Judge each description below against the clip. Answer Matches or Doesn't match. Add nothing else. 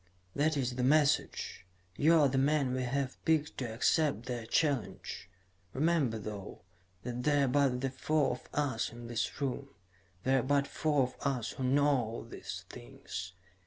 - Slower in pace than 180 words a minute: Matches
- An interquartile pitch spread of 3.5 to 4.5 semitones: Doesn't match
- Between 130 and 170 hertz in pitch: Matches